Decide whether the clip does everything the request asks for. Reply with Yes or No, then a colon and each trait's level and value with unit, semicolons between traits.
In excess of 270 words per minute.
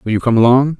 Yes: fast, 300 wpm